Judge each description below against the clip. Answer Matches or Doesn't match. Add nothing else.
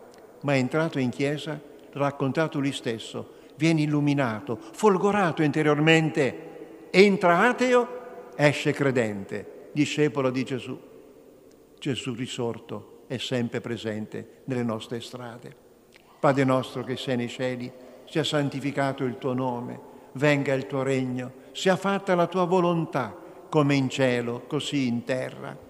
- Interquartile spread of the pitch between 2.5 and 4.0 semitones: Matches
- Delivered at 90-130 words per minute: Matches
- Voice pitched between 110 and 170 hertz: Matches